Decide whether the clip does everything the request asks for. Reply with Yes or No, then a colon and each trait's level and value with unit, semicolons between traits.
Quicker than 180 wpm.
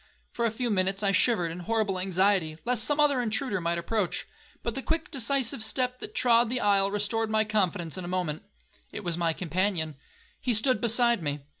Yes: average, 190 wpm